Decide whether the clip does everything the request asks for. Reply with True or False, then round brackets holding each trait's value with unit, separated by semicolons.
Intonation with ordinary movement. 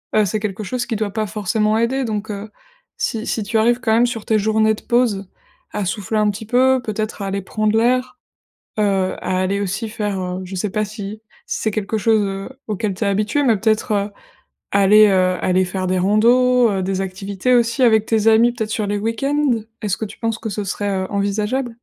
False (2.3 semitones)